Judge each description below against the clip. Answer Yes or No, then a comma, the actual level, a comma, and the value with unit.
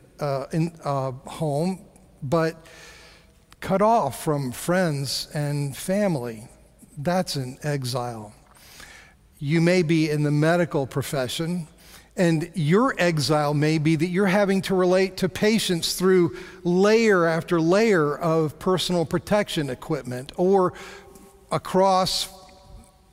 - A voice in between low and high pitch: Yes, medium, 165 Hz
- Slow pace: Yes, slow, 110 wpm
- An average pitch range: Yes, average, 4.2 semitones